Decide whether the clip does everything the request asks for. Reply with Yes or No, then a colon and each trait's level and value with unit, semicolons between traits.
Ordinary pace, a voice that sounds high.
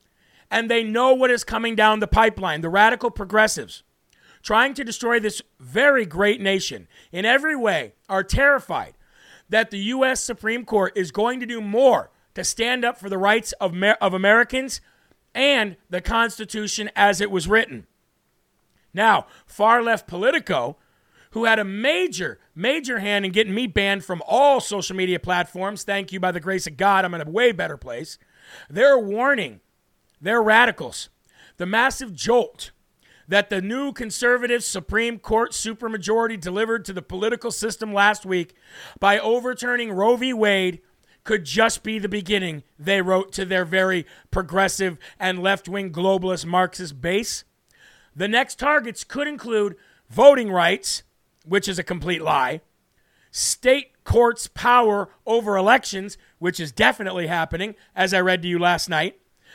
Yes: average, 155 wpm; high, 210 Hz